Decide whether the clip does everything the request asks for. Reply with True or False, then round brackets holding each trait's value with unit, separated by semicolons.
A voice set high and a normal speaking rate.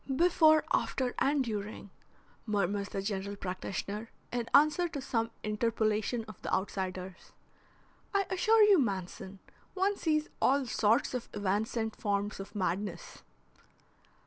False (215 Hz; 120 wpm)